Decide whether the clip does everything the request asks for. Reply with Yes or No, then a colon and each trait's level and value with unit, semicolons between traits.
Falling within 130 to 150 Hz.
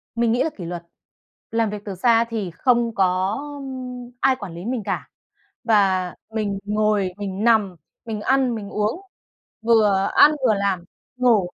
No: high, 215 Hz